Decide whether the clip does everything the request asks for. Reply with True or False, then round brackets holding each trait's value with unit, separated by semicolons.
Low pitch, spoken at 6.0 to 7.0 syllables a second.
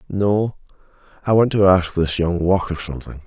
False (95 Hz; 5.2 syllables/s)